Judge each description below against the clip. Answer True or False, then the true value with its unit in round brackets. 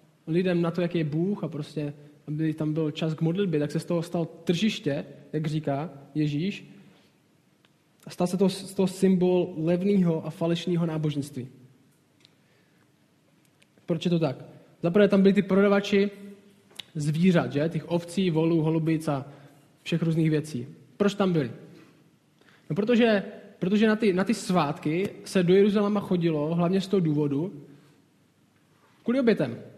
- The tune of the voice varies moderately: True (3.8 semitones)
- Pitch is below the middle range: False (165 Hz)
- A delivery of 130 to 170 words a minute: True (145 wpm)